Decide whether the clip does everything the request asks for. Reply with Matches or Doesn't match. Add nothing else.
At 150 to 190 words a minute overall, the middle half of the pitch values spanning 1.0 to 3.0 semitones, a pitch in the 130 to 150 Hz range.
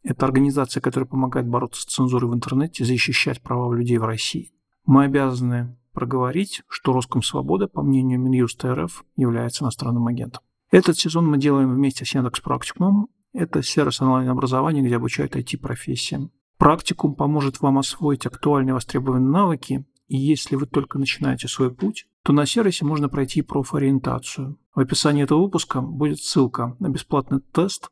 Matches